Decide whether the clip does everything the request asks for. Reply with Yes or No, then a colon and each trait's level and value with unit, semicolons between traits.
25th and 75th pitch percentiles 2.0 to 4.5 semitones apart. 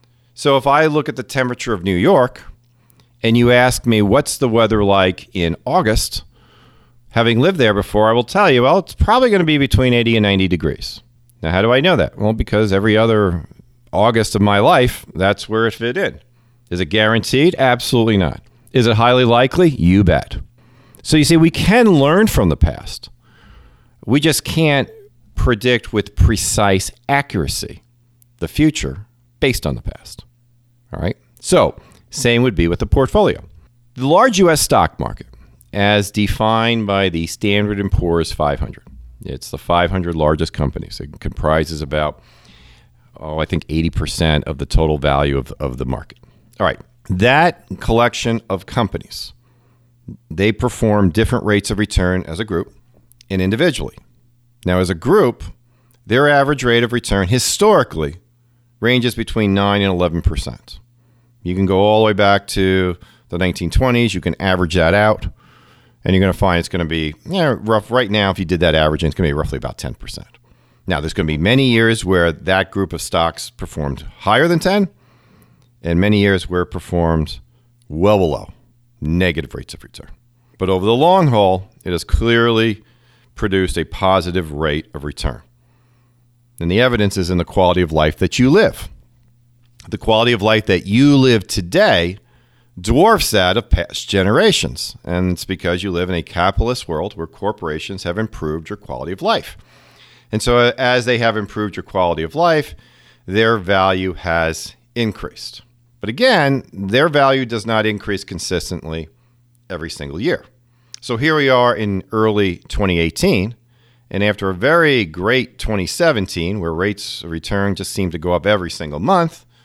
No: average, 5.1 semitones